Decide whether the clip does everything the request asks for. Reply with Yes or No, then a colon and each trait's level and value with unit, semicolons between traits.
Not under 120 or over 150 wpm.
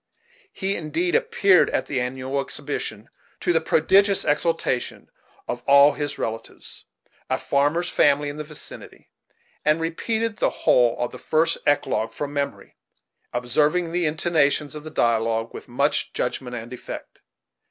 Yes: average, 140 wpm